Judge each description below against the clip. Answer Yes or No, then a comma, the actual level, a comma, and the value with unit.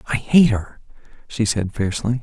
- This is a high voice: No, low, 115 Hz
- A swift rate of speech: No, average, 160 wpm